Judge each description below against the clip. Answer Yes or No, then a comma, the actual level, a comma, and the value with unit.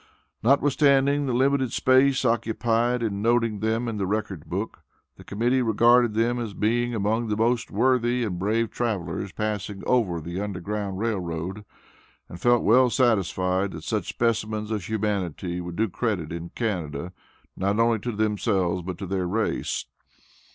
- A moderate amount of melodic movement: Yes, average, 3.7 semitones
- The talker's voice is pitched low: Yes, low, 110 Hz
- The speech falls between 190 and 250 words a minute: No, average, 155 wpm